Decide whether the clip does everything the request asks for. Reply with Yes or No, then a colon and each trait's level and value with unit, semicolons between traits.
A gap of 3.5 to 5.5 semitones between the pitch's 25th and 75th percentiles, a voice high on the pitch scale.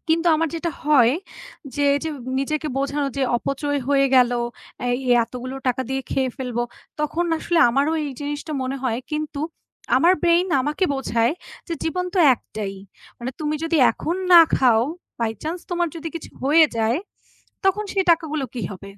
Yes: average, 4.2 semitones; very high, 290 Hz